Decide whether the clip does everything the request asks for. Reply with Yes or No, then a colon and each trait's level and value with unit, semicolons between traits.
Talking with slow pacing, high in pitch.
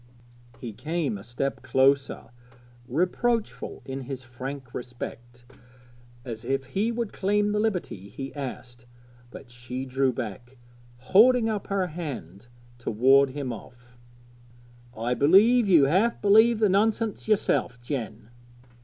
No: slow, 125 wpm; low, 135 Hz